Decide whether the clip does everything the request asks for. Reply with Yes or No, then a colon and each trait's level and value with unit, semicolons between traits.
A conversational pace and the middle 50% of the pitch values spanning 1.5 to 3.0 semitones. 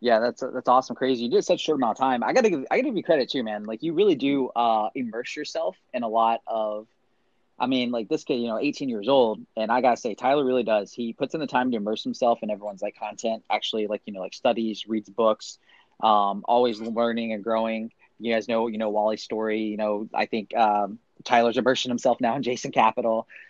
No: fast, 245 wpm; narrow, 2.6 semitones